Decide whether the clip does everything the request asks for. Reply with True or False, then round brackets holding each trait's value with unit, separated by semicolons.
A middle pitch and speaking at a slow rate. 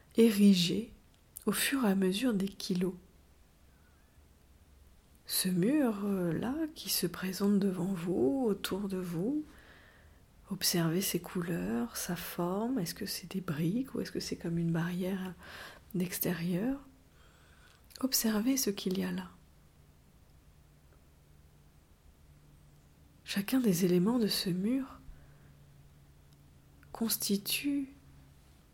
True (180 Hz; 100 wpm)